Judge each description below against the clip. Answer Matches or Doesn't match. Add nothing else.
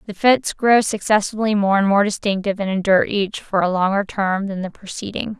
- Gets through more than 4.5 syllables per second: Matches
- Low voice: Doesn't match